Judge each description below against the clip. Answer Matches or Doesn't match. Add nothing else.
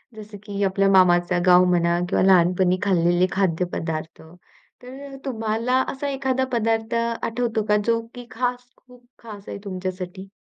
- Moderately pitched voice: Doesn't match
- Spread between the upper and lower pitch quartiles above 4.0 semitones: Matches